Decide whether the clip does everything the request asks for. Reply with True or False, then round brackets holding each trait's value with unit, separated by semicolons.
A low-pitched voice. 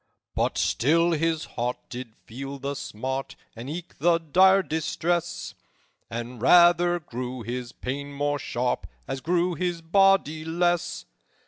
False (155 Hz)